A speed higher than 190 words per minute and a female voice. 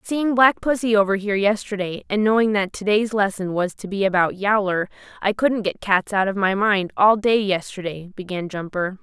Yes: average, 200 wpm; female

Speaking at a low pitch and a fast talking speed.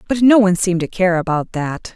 No: medium, 185 Hz; fast, 245 wpm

